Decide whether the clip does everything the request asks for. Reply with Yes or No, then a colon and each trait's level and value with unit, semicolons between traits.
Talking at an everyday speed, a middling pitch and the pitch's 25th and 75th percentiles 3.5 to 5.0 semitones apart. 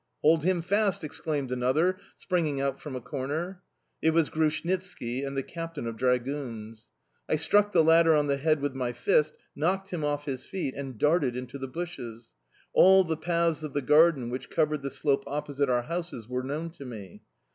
Yes: average, 190 wpm; medium, 145 Hz; average, 4.3 semitones